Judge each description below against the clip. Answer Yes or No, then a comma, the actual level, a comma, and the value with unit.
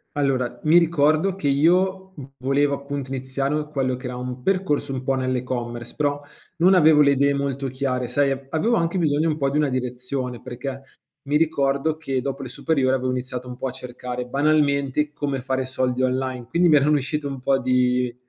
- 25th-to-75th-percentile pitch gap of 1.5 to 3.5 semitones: Yes, average, 2.7 semitones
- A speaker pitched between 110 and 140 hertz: Yes, low, 135 Hz